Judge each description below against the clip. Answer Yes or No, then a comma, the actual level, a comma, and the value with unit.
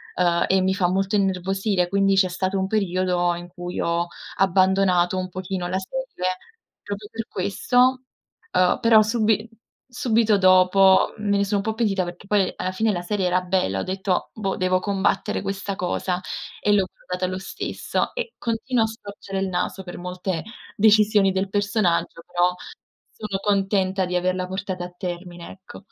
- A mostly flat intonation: Yes, narrow, 2.0 semitones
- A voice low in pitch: No, high, 190 Hz